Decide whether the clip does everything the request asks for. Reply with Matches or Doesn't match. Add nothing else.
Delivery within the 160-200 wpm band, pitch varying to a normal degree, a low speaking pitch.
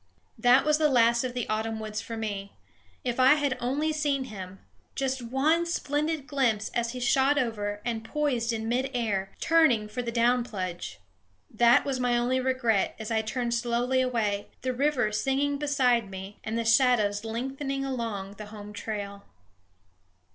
Doesn't match